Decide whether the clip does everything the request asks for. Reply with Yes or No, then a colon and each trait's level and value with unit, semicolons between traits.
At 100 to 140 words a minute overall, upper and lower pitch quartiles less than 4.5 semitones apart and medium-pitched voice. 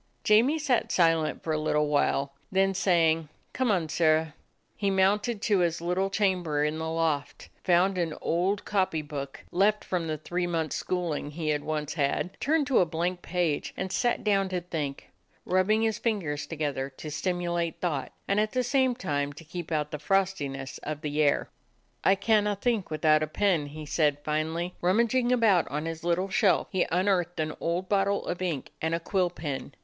No: average, 190 wpm; average, 4.1 semitones; medium, 175 Hz